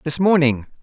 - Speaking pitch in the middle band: Yes, medium, 150 Hz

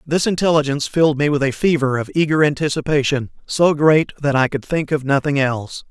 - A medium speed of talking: Yes, average, 195 wpm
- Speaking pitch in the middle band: Yes, medium, 145 Hz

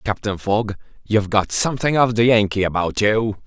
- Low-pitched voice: Yes, low, 105 Hz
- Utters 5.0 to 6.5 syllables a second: Yes, 5.3 syllables/s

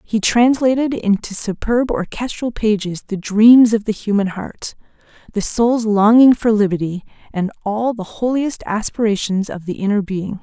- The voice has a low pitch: No, high, 215 Hz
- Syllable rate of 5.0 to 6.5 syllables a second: No, 4.5 syllables/s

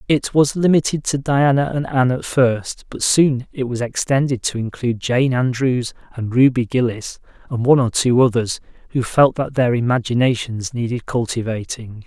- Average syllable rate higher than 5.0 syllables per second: No, 4.9 syllables/s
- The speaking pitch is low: Yes, low, 125 Hz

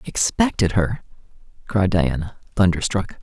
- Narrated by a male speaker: Yes, male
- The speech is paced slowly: Yes, slow, 95 wpm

